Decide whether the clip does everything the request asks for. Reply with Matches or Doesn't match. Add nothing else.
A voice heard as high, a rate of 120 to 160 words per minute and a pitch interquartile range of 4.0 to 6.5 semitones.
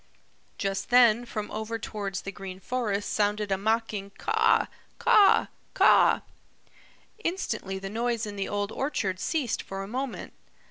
Doesn't match